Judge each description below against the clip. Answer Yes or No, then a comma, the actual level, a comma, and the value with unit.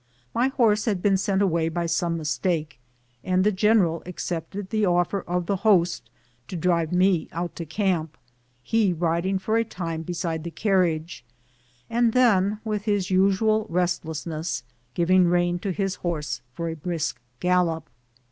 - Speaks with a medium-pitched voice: Yes, medium, 180 Hz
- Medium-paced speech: Yes, average, 155 wpm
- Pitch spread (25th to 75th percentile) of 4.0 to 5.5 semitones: No, average, 3.1 semitones